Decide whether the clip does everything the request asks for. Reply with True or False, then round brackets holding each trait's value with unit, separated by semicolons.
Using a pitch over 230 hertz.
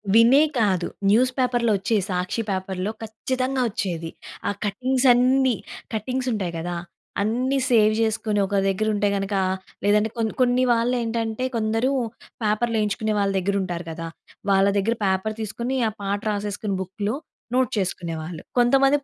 False (215 Hz)